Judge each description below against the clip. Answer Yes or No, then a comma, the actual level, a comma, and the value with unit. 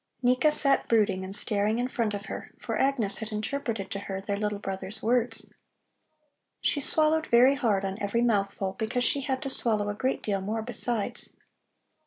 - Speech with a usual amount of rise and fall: Yes, average, 3.7 semitones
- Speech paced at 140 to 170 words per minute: No, average, 180 wpm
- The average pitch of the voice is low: No, high, 220 Hz